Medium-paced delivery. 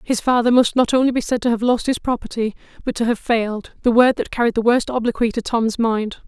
No: fast, 240 wpm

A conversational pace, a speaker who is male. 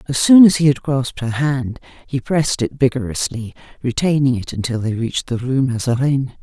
No: average, 185 wpm; female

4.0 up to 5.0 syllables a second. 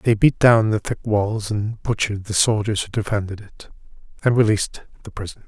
No: 5.5 syllables/s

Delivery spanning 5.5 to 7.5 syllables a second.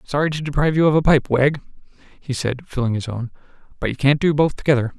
Yes: 6.4 syllables/s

